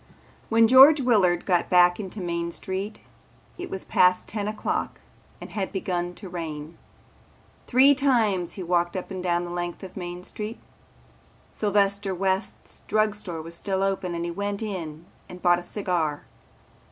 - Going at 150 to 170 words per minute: Yes, average, 160 wpm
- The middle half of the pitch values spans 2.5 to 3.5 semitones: Yes, average, 3.0 semitones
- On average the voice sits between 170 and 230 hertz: Yes, medium, 185 Hz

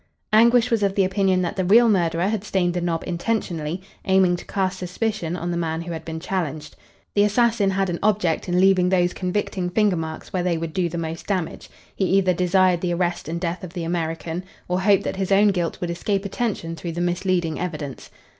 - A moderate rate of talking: No, fast, 215 wpm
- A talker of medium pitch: Yes, medium, 180 Hz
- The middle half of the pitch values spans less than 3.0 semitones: Yes, narrow, 2.4 semitones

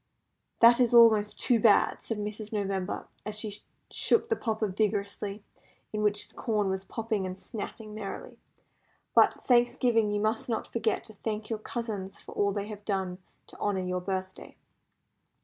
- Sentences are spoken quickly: No, average, 165 wpm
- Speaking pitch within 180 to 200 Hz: No, high, 210 Hz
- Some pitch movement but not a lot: No, narrow, 2.1 semitones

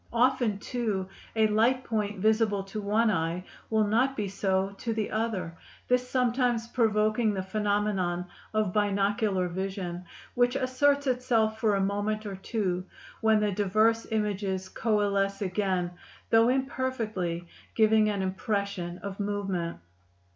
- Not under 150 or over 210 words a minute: No, slow, 135 wpm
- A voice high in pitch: Yes, high, 210 Hz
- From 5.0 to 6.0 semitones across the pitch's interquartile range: No, average, 2.8 semitones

